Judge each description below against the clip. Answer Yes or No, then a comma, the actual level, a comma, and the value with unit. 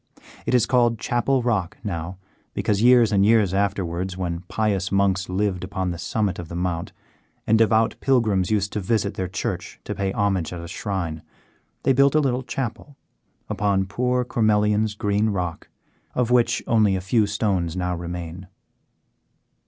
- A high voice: No, low, 100 Hz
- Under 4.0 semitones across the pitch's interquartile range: Yes, average, 3.6 semitones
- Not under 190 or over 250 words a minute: No, average, 160 wpm